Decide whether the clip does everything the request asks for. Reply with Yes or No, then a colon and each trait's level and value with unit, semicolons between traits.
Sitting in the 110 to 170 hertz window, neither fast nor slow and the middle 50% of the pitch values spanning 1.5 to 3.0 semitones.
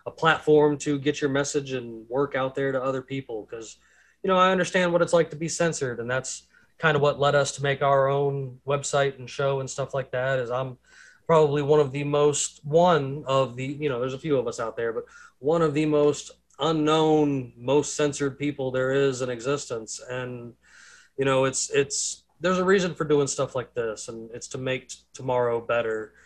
No: medium, 140 Hz; fast, 215 wpm; narrow, 2.5 semitones